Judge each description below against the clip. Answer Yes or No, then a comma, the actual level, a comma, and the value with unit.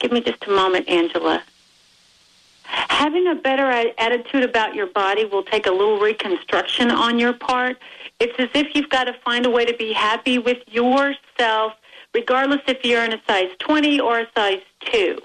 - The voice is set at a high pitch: Yes, high, 245 Hz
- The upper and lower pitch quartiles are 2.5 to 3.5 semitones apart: No, average, 4.3 semitones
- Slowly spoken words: No, average, 180 wpm